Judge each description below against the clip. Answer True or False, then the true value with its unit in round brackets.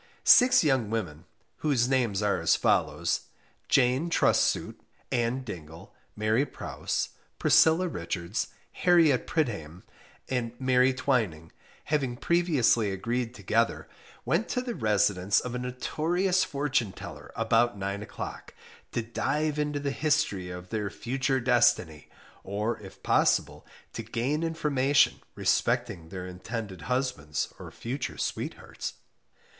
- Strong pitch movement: True (5.7 semitones)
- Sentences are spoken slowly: True (120 wpm)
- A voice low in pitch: True (120 Hz)